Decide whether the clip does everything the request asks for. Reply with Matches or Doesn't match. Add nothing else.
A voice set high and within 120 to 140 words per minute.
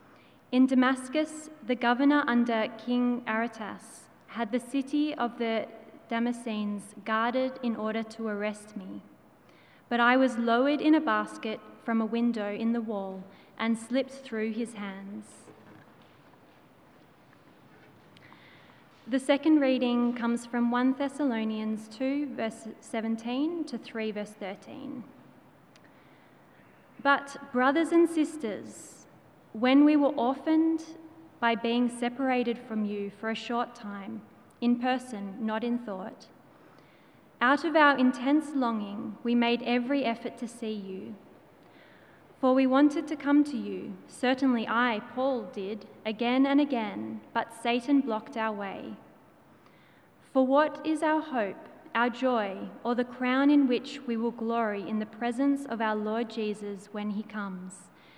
Matches